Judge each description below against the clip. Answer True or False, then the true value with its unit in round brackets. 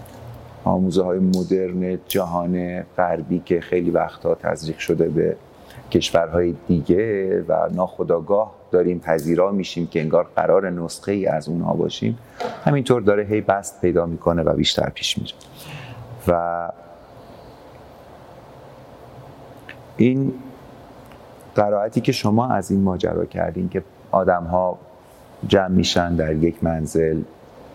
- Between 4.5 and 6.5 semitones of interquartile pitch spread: True (5.2 semitones)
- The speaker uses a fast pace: False (115 wpm)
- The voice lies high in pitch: False (90 Hz)